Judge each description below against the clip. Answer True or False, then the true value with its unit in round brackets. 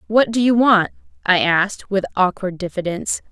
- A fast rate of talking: False (165 wpm)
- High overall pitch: True (195 Hz)